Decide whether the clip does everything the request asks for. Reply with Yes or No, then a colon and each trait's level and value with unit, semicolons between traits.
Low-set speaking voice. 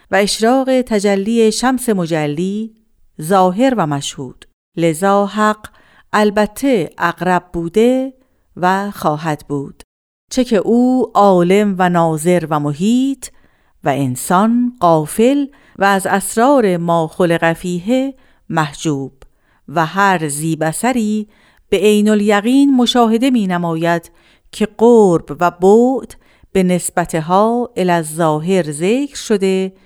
No: high, 195 Hz